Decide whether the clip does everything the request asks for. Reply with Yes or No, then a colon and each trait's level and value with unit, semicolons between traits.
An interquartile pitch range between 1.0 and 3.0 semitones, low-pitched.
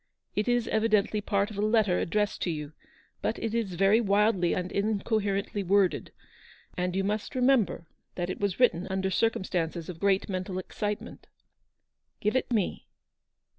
No: average, 2.7 semitones; high, 200 Hz